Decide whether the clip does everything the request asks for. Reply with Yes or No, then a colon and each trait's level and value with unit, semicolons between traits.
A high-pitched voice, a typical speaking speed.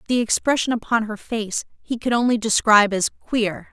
Yes: high, 225 Hz; average, 175 wpm